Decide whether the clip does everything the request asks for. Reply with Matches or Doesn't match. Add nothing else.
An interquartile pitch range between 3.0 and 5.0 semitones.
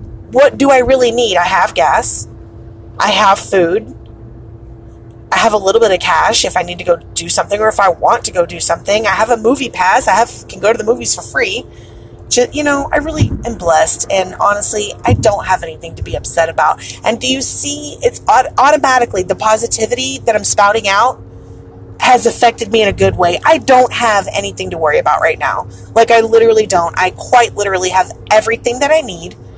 Doesn't match